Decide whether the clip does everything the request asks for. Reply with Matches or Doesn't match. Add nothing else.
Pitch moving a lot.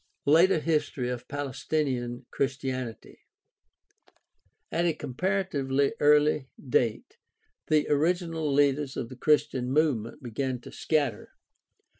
Doesn't match